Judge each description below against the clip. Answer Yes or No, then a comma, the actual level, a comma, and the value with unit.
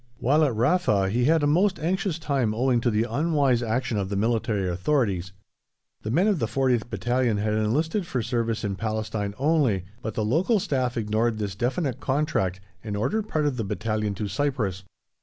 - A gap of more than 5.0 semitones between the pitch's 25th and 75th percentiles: Yes, wide, 5.4 semitones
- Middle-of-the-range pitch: No, low, 120 Hz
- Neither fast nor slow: Yes, average, 185 wpm